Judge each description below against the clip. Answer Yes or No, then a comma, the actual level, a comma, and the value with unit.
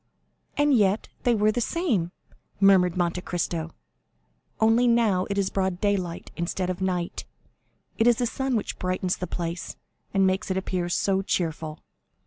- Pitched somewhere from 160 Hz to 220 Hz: Yes, high, 190 Hz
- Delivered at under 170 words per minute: Yes, average, 155 wpm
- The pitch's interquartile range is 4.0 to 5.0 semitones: No, average, 3.4 semitones